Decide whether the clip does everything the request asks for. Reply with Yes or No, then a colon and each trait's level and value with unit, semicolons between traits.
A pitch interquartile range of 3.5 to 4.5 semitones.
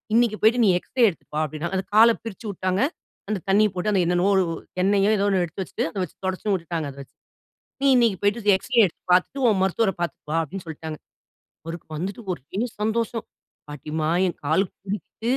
Yes: average, 3.9 semitones